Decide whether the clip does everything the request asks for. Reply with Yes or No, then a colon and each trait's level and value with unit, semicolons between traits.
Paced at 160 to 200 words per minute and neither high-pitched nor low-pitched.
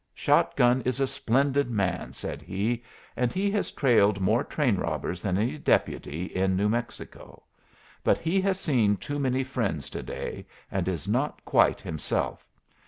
No: average, 165 wpm; low, 120 Hz